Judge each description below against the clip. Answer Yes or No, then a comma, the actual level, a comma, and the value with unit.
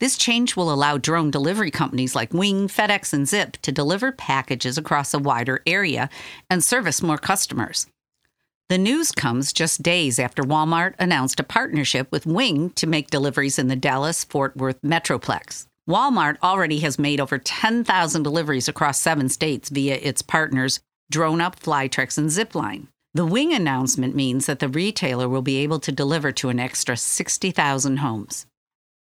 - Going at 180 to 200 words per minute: No, average, 160 wpm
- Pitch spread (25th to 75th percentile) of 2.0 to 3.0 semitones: No, average, 3.8 semitones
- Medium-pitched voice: Yes, medium, 150 Hz